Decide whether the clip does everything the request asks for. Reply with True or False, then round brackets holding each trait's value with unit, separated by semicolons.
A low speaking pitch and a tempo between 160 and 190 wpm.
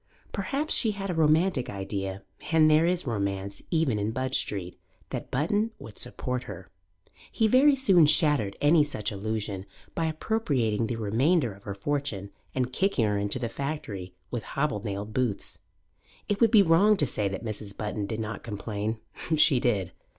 True (120 Hz; 165 wpm)